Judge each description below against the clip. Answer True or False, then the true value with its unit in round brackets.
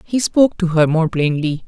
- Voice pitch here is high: False (175 Hz)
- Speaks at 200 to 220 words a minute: True (215 wpm)